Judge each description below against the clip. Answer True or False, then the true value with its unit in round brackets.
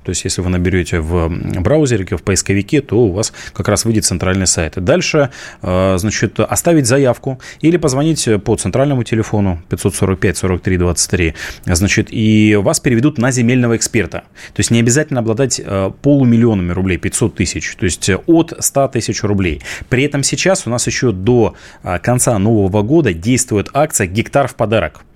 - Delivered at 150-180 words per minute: True (155 wpm)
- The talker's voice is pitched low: True (110 Hz)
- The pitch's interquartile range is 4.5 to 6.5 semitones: True (5.0 semitones)